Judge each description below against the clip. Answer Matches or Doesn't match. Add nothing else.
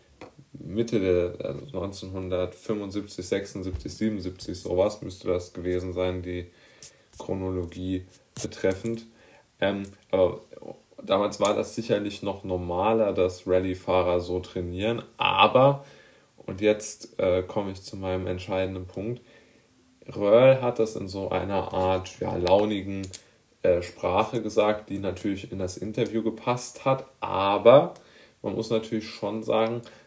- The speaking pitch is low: Matches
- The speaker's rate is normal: Doesn't match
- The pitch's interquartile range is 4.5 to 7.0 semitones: Doesn't match